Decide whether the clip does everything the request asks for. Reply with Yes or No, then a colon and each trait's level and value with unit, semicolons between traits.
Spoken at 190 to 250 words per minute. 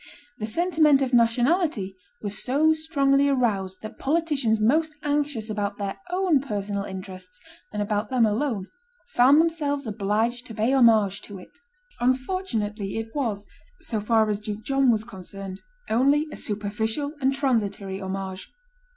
No: average, 140 wpm